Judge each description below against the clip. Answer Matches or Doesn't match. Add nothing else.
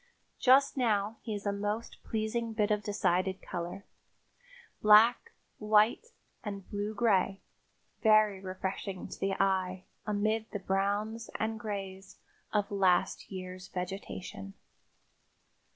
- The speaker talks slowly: Matches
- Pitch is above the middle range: Matches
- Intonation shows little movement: Matches